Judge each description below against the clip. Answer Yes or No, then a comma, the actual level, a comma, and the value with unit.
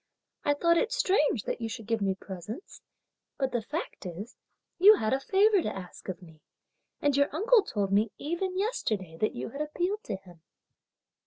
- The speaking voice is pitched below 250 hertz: No, very high, 260 Hz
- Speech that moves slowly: No, average, 185 wpm